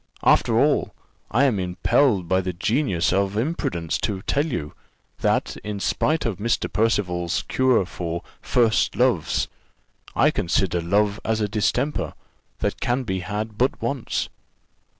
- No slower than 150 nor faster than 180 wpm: No, average, 140 wpm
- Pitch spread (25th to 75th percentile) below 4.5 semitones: No, average, 4.9 semitones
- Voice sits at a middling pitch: No, low, 105 Hz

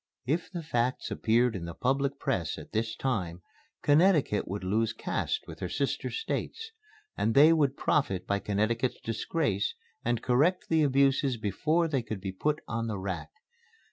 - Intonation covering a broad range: Yes, wide, 5.8 semitones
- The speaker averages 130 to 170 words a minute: Yes, average, 165 wpm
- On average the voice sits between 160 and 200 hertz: No, low, 120 Hz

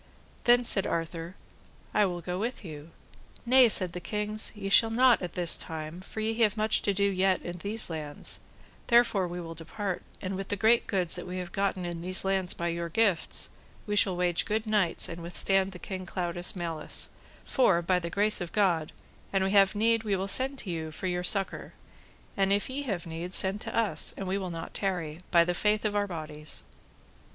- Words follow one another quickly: Yes, fast, 210 wpm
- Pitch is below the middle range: No, high, 190 Hz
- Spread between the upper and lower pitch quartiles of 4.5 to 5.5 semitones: No, average, 3.2 semitones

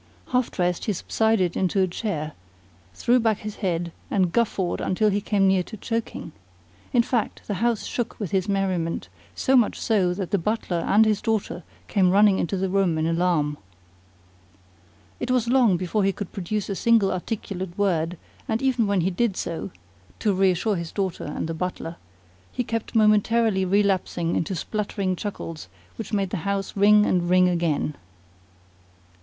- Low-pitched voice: No, high, 195 Hz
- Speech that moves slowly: No, average, 170 wpm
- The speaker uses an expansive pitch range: No, average, 3.3 semitones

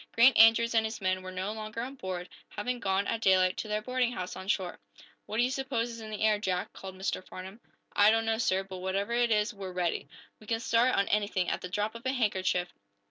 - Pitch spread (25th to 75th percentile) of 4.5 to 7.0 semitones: No, average, 3.5 semitones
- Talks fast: Yes, fast, 245 wpm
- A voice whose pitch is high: Yes, high, 210 Hz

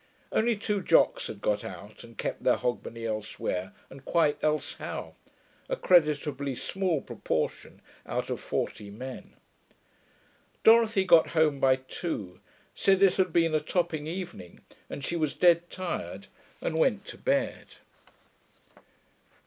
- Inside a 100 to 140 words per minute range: Yes, slow, 135 wpm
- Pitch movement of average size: No, wide, 6.4 semitones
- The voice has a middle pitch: Yes, medium, 155 Hz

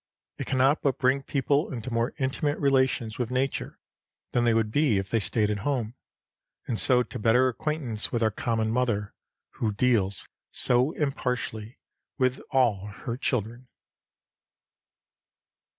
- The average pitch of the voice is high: No, low, 125 Hz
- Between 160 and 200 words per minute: No, average, 140 wpm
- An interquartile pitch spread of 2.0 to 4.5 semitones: Yes, average, 3.1 semitones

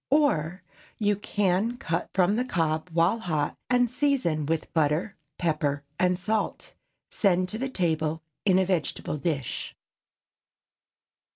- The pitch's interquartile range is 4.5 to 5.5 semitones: Yes, average, 5.0 semitones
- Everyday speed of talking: No, slow, 120 wpm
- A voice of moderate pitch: Yes, medium, 180 Hz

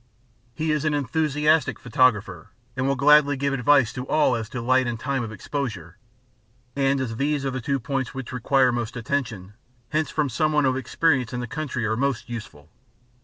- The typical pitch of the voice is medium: No, low, 130 Hz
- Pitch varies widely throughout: No, average, 3.2 semitones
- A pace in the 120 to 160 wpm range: No, average, 190 wpm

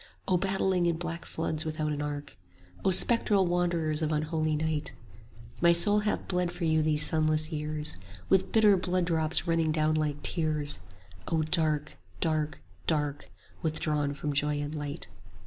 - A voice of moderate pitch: Yes, medium, 155 Hz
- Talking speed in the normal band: Yes, average, 160 wpm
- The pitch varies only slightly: Yes, narrow, 2.3 semitones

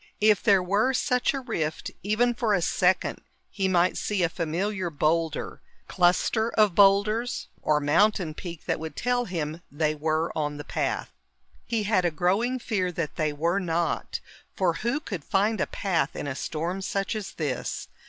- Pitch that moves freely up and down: No, average, 4.7 semitones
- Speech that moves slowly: No, average, 175 wpm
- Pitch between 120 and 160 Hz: No, medium, 185 Hz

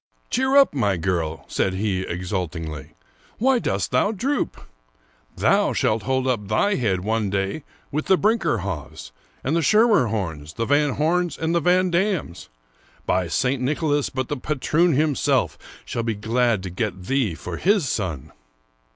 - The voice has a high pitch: No, low, 125 Hz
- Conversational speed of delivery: Yes, average, 160 wpm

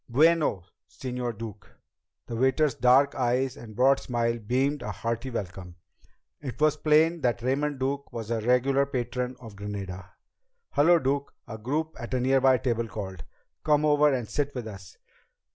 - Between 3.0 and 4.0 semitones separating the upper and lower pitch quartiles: Yes, average, 3.5 semitones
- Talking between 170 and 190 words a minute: No, average, 160 wpm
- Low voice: Yes, low, 125 Hz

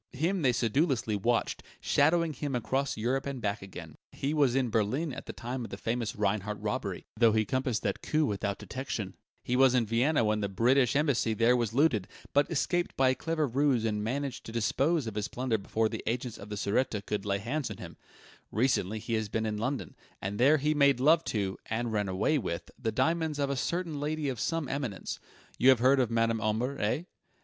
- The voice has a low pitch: Yes, low, 125 Hz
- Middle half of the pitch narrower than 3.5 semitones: No, average, 4.4 semitones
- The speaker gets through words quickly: Yes, fast, 210 wpm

